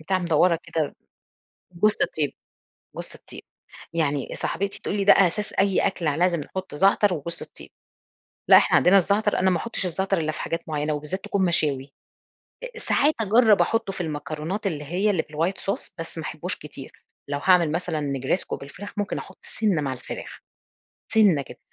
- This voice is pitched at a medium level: Yes, medium, 175 Hz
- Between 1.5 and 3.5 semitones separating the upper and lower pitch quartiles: No, average, 4.4 semitones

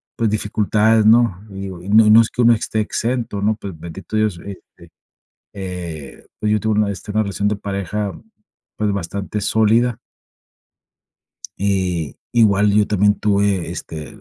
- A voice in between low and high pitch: No, low, 105 Hz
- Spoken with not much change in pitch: Yes, narrow, 2.0 semitones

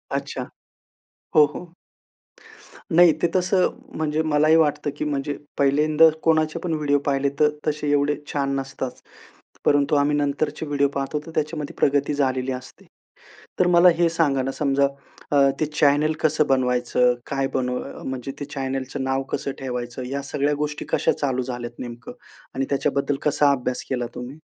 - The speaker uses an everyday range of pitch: No, narrow, 2.1 semitones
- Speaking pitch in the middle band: Yes, medium, 145 Hz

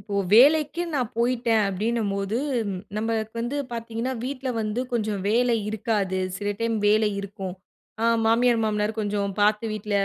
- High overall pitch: Yes, high, 220 Hz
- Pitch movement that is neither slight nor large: No, narrow, 2.3 semitones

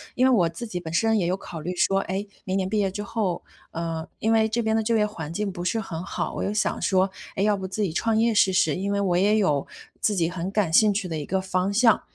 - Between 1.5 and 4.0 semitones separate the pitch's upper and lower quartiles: Yes, average, 3.4 semitones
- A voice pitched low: No, high, 195 Hz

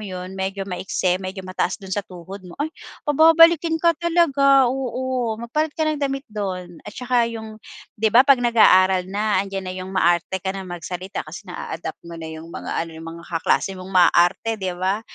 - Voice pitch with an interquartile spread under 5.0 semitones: No, wide, 5.6 semitones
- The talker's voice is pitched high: Yes, high, 195 Hz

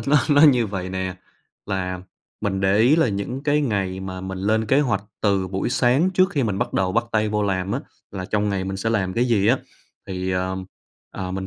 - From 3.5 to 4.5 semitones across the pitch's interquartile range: Yes, average, 4.1 semitones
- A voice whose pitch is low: Yes, low, 100 Hz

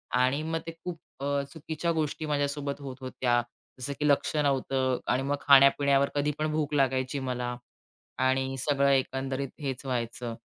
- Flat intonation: Yes, narrow, 1.9 semitones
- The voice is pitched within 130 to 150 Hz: Yes, medium, 140 Hz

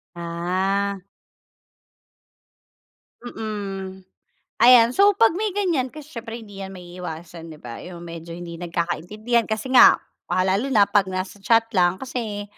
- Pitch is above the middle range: Yes, high, 195 Hz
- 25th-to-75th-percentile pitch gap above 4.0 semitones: Yes, average, 4.7 semitones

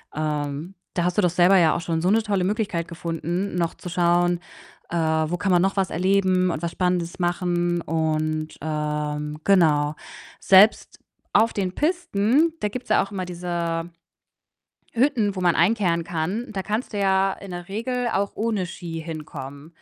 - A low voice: No, medium, 175 Hz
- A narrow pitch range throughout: No, average, 3.3 semitones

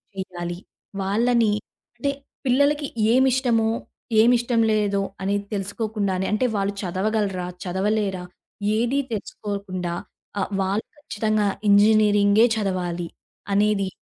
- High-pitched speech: Yes, high, 205 Hz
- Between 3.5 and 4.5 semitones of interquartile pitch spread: No, average, 2.7 semitones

